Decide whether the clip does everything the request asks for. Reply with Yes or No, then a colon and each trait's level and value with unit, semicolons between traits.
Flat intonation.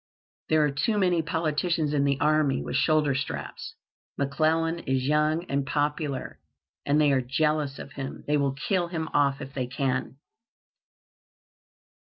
Yes: narrow, 2.3 semitones